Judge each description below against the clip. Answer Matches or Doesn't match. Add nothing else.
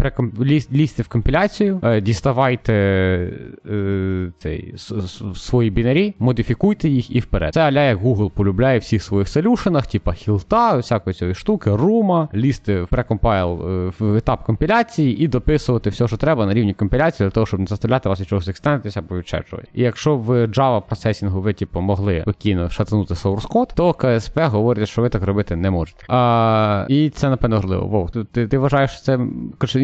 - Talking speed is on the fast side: Matches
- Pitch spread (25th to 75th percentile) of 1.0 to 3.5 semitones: Doesn't match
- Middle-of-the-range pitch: Doesn't match